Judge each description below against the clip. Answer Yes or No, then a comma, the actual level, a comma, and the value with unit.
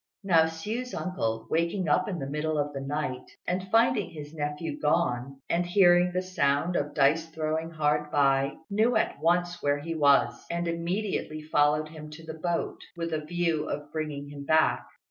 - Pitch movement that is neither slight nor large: Yes, average, 3.0 semitones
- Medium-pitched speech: Yes, medium, 160 Hz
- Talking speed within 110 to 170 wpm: No, average, 180 wpm